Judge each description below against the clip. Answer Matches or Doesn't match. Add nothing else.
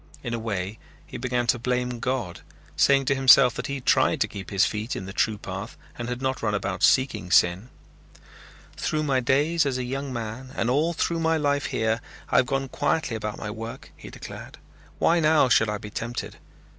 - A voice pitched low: Matches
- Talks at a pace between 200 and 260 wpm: Matches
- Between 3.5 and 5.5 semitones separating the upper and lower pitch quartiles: Matches